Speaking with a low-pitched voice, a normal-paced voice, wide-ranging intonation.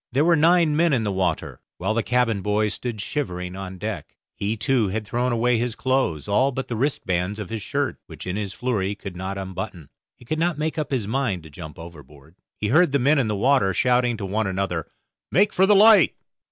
No: low, 110 Hz; fast, 230 wpm; wide, 5.9 semitones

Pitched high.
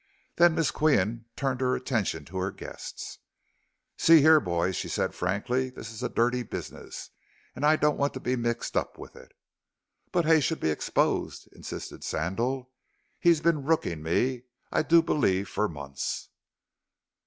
No: low, 125 Hz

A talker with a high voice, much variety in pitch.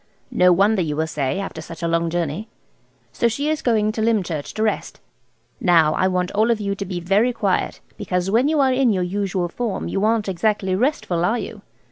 No: high, 195 Hz; average, 4.1 semitones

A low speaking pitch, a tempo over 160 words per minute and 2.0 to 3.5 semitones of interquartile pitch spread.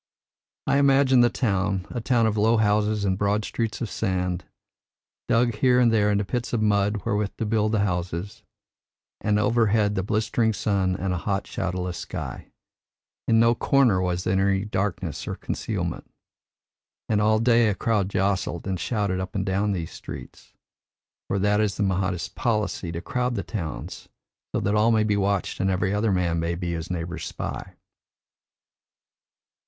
Yes: low, 105 Hz; average, 170 wpm; average, 2.9 semitones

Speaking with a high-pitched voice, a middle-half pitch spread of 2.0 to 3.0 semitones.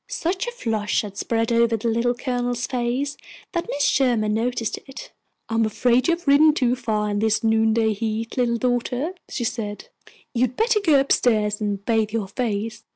Yes: high, 235 Hz; narrow, 2.6 semitones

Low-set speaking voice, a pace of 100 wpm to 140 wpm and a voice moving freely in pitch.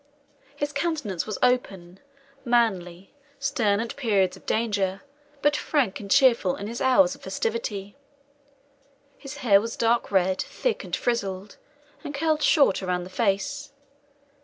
No: high, 230 Hz; slow, 135 wpm; wide, 6.2 semitones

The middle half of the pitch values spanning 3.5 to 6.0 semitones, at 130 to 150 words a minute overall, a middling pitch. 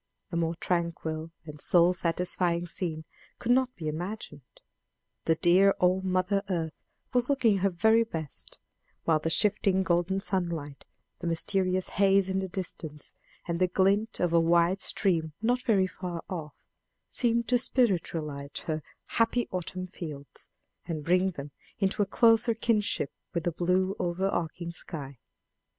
No: average, 3.1 semitones; average, 145 wpm; medium, 180 Hz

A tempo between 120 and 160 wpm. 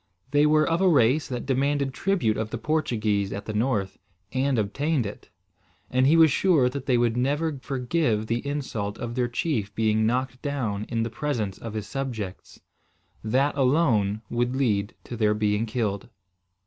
No: average, 175 wpm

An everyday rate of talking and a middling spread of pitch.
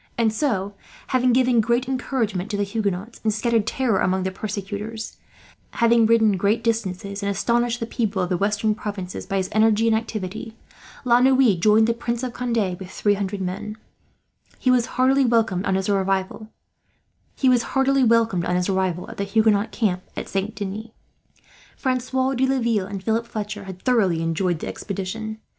Yes: average, 160 wpm; average, 3.3 semitones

